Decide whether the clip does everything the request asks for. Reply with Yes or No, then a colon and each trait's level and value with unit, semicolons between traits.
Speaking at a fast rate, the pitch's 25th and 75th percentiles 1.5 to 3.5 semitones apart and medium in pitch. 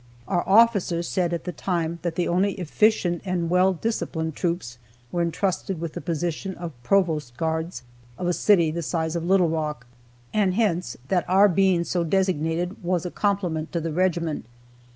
No: average, 170 wpm; narrow, 2.5 semitones; medium, 175 Hz